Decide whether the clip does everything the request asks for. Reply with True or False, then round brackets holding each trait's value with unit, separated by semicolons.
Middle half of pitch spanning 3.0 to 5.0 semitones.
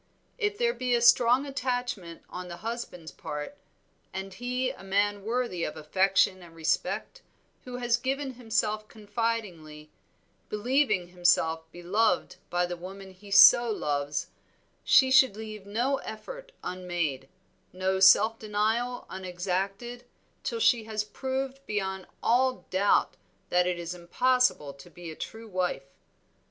False (5.4 semitones)